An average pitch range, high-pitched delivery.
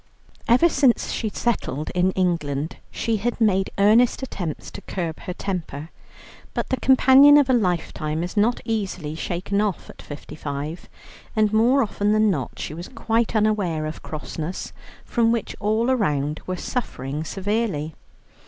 No: wide, 6.2 semitones; high, 200 Hz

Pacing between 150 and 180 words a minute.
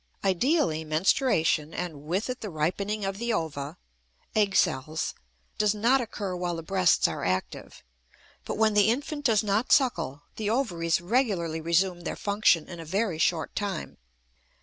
Yes: average, 155 wpm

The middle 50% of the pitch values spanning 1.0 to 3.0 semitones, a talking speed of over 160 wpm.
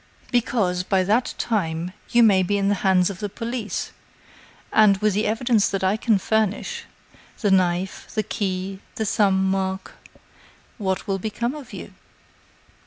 No: narrow, 2.5 semitones; average, 155 wpm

